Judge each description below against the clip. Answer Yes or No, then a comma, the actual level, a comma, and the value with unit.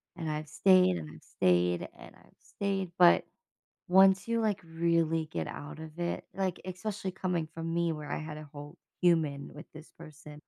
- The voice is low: No, medium, 165 Hz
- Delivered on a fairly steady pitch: No, average, 3.3 semitones